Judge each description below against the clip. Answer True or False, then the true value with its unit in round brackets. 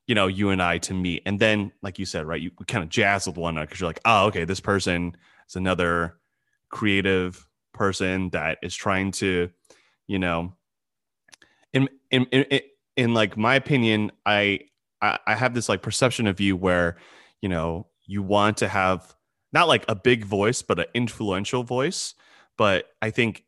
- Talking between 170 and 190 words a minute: True (180 wpm)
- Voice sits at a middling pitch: False (100 Hz)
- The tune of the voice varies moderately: True (3.5 semitones)